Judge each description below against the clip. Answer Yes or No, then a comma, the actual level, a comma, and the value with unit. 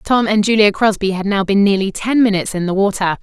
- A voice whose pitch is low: No, high, 200 Hz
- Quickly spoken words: Yes, fast, 240 wpm